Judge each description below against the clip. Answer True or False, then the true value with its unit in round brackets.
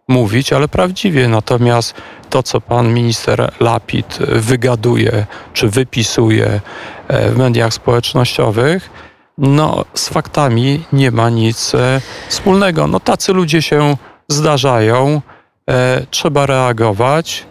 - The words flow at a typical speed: False (105 wpm)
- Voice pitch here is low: True (130 Hz)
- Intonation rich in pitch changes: False (4.1 semitones)